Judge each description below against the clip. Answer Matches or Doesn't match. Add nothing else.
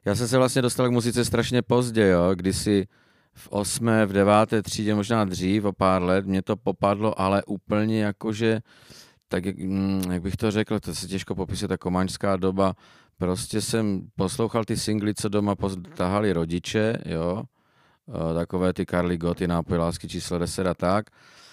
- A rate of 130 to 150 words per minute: Doesn't match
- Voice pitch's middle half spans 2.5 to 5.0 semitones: Matches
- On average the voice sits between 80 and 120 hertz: Matches